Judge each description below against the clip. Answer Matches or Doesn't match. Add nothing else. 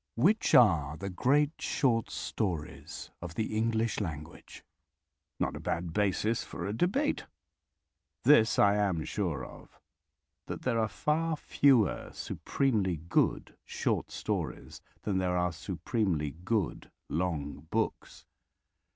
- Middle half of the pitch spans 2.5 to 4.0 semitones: Doesn't match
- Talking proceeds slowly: Matches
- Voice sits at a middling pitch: Doesn't match